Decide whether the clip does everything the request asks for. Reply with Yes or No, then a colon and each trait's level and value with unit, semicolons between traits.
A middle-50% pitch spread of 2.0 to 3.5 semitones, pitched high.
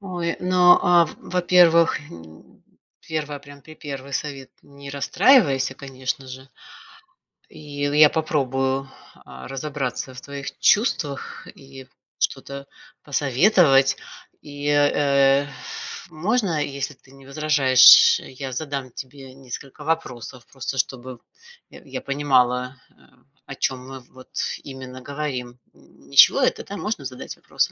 No: narrow, 2.5 semitones; medium, 140 Hz